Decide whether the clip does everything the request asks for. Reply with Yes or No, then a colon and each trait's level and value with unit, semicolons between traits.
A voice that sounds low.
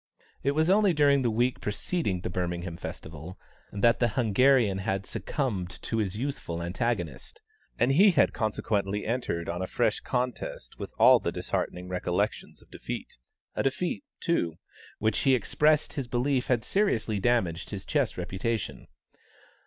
Yes: low, 115 Hz